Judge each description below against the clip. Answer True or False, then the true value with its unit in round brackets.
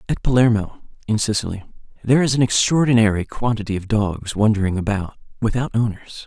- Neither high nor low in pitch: False (110 Hz)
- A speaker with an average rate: True (145 wpm)